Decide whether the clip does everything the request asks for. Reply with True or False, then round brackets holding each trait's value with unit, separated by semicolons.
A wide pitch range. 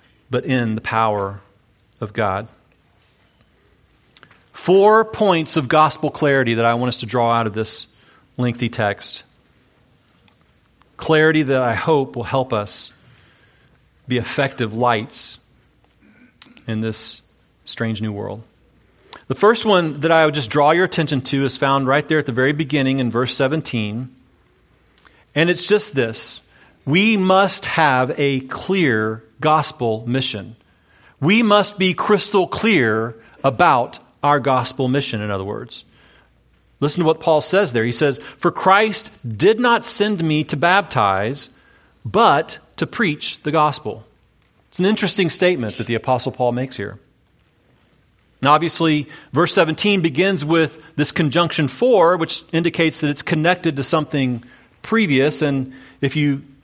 True (5.8 semitones)